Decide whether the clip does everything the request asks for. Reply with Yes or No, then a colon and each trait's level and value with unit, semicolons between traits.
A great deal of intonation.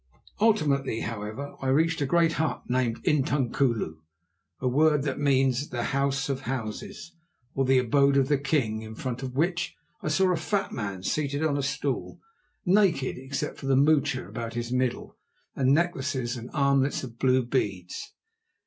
No: average, 3.0 semitones